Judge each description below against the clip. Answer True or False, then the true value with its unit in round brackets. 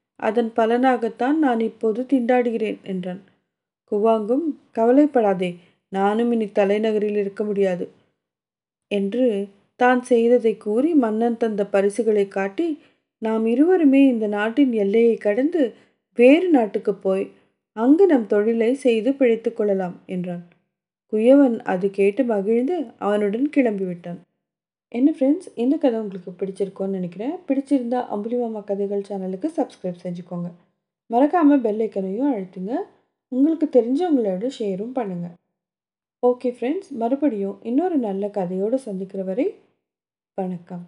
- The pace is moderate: True (105 wpm)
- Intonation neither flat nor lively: True (4.5 semitones)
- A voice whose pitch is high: True (225 Hz)